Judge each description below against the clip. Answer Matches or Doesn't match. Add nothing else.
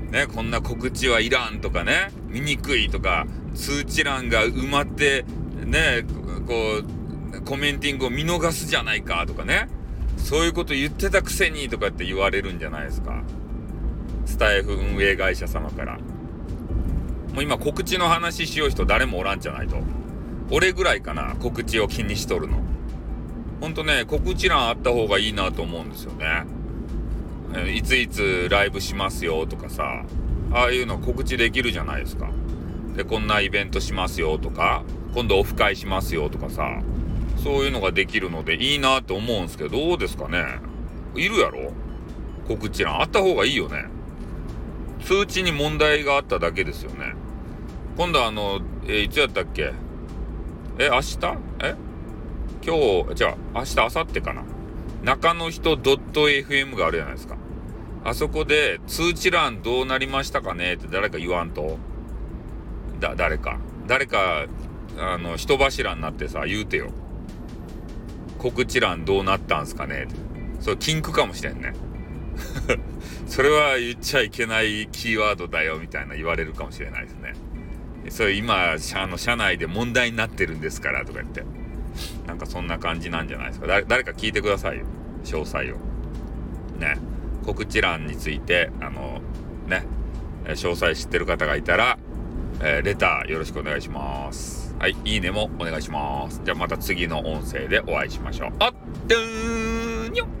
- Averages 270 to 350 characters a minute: Matches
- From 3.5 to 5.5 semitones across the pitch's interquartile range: Doesn't match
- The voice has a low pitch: Matches